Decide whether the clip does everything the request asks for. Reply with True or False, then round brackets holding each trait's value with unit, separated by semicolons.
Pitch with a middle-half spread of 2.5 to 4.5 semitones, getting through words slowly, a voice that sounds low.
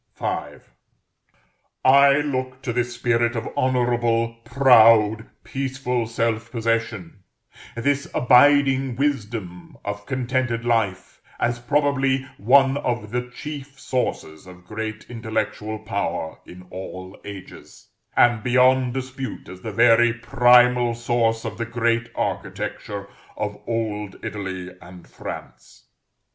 True (3.0 semitones; 110 wpm; 120 Hz)